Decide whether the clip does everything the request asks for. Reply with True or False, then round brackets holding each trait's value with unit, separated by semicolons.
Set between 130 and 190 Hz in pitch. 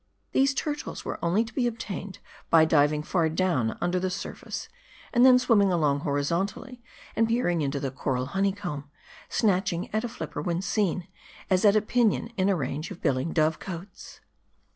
True (185 Hz)